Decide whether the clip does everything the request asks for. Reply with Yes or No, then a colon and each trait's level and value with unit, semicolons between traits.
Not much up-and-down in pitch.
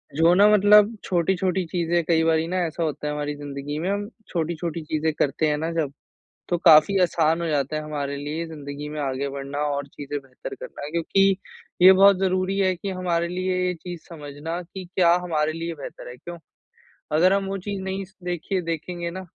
No: average, 3.6 semitones